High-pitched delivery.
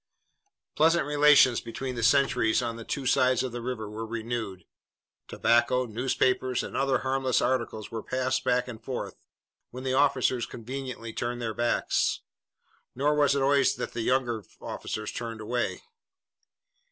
No: low, 125 Hz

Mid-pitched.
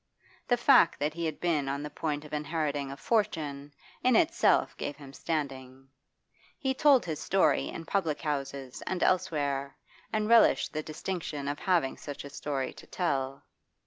Yes: medium, 150 Hz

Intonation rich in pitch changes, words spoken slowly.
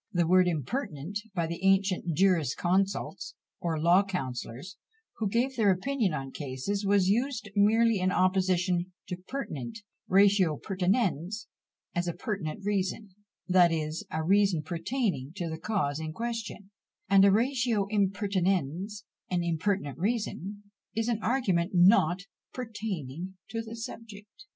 No: average, 3.5 semitones; slow, 130 wpm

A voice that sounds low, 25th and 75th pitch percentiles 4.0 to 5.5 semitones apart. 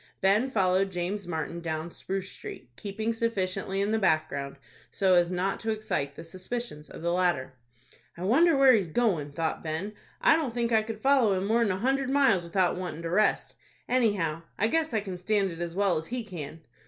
No: high, 195 Hz; average, 4.7 semitones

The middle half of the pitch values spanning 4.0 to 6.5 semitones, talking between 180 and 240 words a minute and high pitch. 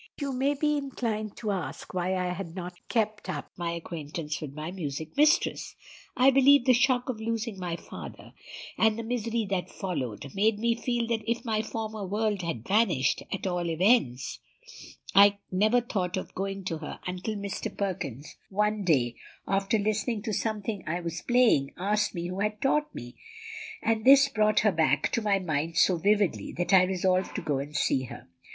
Yes: average, 4.6 semitones; average, 185 wpm; high, 200 Hz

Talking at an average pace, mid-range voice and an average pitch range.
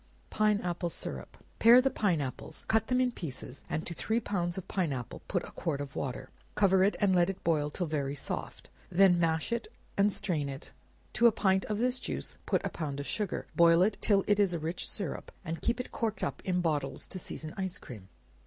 No: fast, 220 wpm; medium, 180 Hz; average, 4.8 semitones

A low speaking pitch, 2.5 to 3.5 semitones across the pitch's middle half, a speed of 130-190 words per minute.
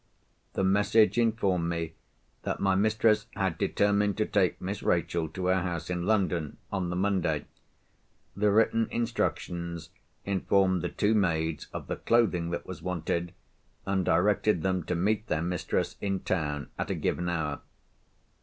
Yes: very low, 95 Hz; average, 3.1 semitones; average, 155 wpm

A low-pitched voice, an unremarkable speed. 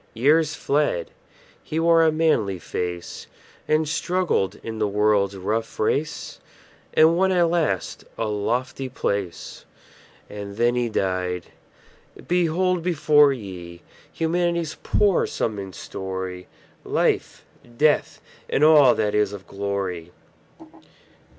No: low, 115 Hz; slow, 115 wpm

